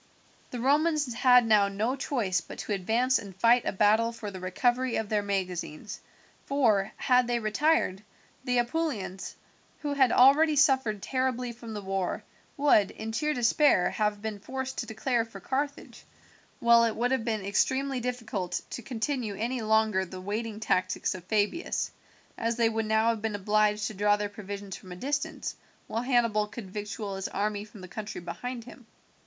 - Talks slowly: No, average, 175 wpm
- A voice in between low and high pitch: No, high, 225 Hz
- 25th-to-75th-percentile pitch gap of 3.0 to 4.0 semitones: Yes, average, 3.5 semitones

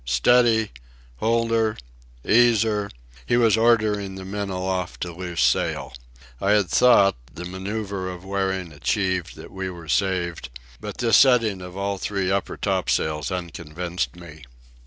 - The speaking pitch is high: No, very low, 95 Hz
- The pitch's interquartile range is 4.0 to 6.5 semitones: No, average, 3.2 semitones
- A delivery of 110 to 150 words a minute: Yes, average, 145 wpm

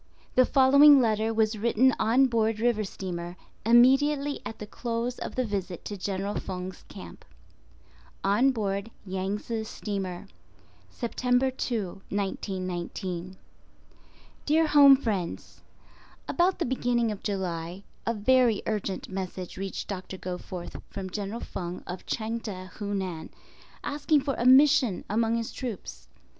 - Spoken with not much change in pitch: No, average, 4.7 semitones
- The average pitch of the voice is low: No, high, 215 Hz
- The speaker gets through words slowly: Yes, slow, 130 wpm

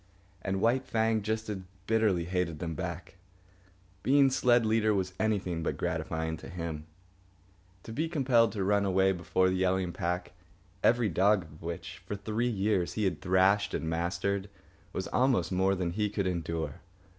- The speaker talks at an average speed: Yes, average, 165 wpm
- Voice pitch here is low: Yes, very low, 95 Hz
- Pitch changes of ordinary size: Yes, average, 3.8 semitones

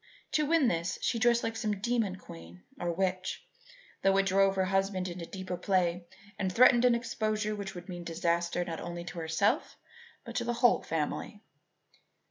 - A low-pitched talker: No, high, 190 Hz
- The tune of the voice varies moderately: Yes, average, 4.3 semitones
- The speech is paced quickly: No, average, 175 wpm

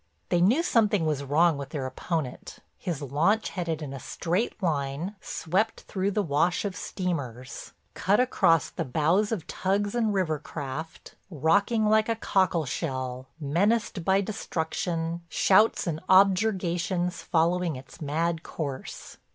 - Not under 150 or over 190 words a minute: No, slow, 135 wpm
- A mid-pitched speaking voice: Yes, medium, 170 Hz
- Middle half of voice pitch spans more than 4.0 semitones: Yes, average, 4.7 semitones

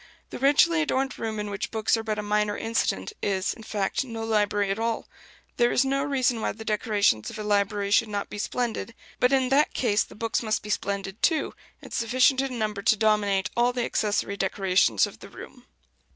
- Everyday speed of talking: No, fast, 210 wpm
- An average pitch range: Yes, average, 3.2 semitones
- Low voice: No, high, 220 Hz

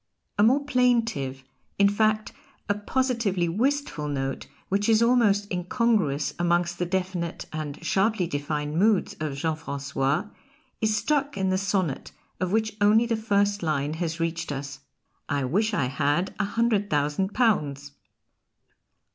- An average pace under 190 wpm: Yes, average, 140 wpm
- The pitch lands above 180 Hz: Yes, high, 190 Hz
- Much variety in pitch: Yes, wide, 6.4 semitones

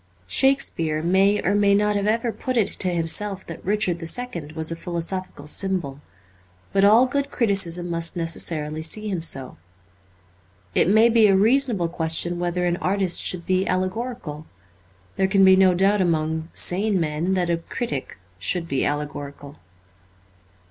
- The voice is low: No, medium, 180 Hz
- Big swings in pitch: No, average, 3.7 semitones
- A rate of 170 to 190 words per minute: No, average, 155 wpm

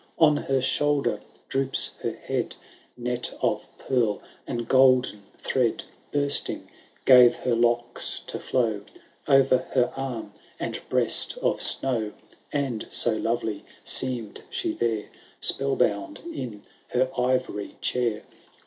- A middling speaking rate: No, slow, 120 wpm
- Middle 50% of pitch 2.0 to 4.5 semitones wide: Yes, average, 2.7 semitones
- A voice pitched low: Yes, low, 125 Hz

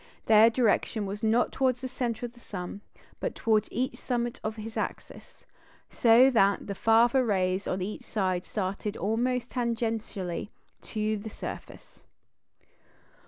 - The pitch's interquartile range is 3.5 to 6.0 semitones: No, average, 2.9 semitones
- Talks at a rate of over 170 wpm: No, average, 140 wpm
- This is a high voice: Yes, high, 220 Hz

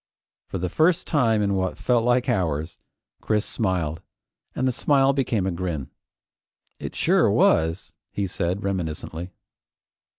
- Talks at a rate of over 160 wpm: No, slow, 135 wpm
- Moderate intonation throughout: No, wide, 6.1 semitones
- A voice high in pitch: No, very low, 95 Hz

